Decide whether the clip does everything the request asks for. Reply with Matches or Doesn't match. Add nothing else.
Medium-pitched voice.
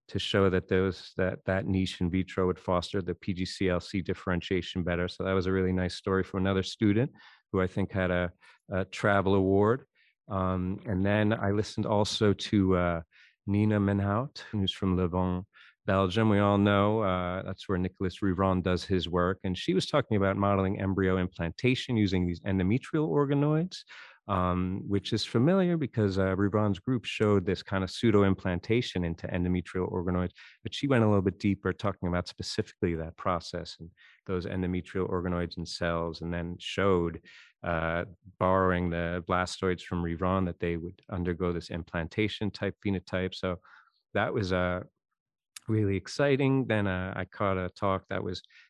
Doesn't match